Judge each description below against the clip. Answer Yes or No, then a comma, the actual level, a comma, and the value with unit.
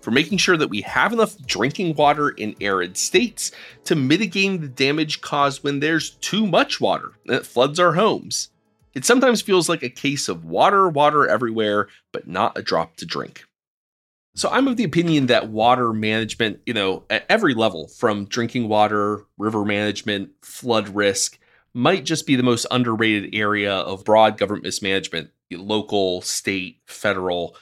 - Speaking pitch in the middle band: No, low, 120 Hz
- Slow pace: No, average, 165 wpm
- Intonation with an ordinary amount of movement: No, wide, 6.6 semitones